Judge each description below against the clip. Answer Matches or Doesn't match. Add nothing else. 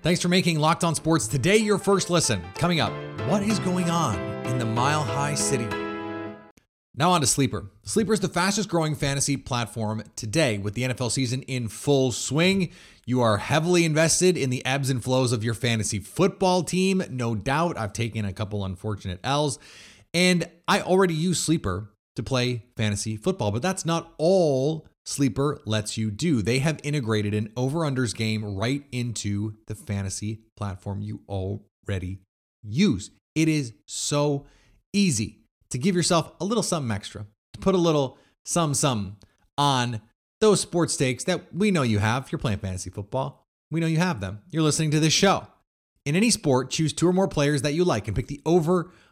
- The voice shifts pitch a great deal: Matches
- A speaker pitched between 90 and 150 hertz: Matches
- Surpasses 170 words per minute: Matches